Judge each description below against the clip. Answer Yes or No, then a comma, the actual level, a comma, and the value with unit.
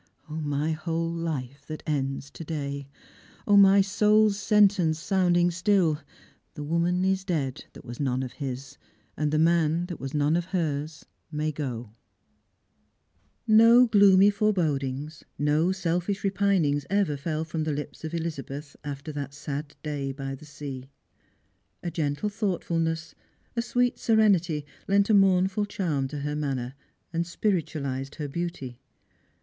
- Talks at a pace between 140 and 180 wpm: Yes, average, 150 wpm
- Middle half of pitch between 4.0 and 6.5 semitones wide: Yes, average, 4.7 semitones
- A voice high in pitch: No, medium, 160 Hz